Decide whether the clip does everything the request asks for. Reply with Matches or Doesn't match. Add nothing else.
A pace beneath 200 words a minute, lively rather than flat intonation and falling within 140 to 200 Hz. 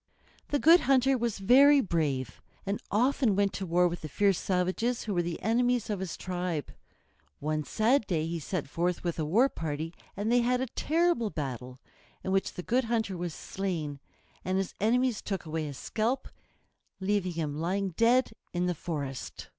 Matches